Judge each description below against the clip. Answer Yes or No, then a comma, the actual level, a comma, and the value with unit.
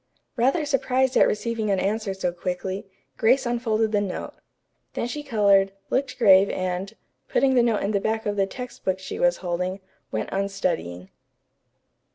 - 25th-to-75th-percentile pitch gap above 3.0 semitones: Yes, average, 3.8 semitones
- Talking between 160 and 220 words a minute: Yes, average, 170 wpm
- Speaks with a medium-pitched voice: No, high, 205 Hz